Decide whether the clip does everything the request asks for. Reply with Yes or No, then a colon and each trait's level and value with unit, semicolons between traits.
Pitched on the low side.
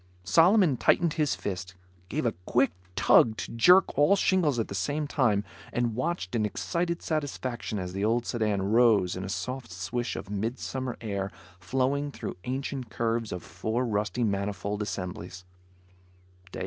Yes: low, 115 Hz